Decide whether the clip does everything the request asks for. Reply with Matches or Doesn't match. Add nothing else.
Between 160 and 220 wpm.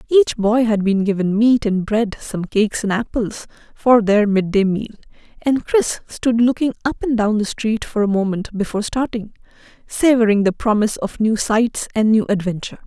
Matches